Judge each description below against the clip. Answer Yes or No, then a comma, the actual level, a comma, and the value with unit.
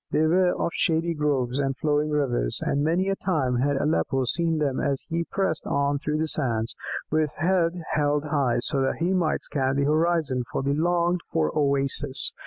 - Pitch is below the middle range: No, medium, 150 Hz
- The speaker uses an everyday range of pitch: Yes, average, 3.4 semitones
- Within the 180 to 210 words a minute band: Yes, average, 190 wpm